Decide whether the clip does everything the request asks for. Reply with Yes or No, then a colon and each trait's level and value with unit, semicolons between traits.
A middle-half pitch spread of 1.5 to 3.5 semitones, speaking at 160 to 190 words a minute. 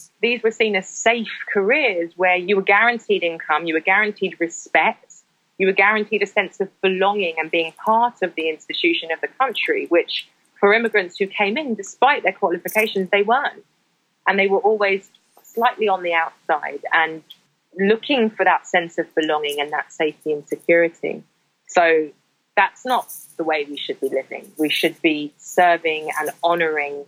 No: average, 4.1 semitones; average, 170 wpm